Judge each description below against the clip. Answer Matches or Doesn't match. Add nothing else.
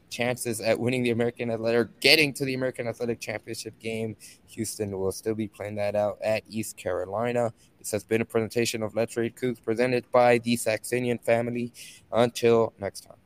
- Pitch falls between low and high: Doesn't match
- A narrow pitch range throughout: Matches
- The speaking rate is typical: Matches